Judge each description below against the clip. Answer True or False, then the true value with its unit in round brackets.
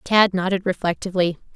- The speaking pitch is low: False (185 Hz)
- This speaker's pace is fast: False (115 wpm)